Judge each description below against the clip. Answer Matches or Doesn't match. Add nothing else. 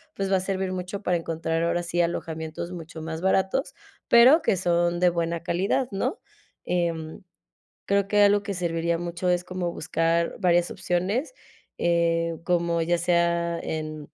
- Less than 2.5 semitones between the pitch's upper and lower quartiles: Matches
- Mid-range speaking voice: Matches